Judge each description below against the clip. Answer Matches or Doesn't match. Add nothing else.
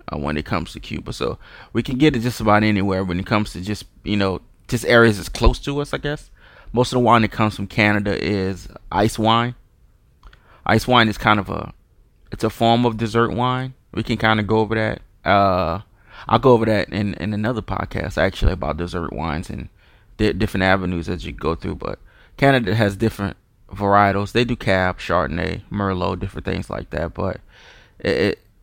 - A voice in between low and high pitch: Doesn't match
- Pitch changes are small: Doesn't match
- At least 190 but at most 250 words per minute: Matches